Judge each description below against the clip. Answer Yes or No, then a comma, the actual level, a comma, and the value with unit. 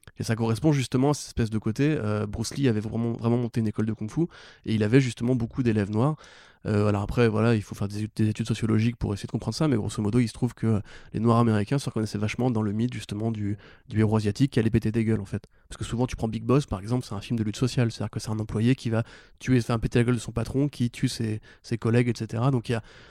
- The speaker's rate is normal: No, fast, 295 wpm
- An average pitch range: No, narrow, 2.3 semitones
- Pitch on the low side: Yes, low, 115 Hz